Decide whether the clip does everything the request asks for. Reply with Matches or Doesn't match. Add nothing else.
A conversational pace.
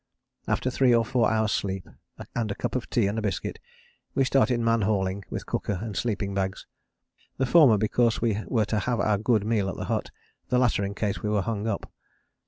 Doesn't match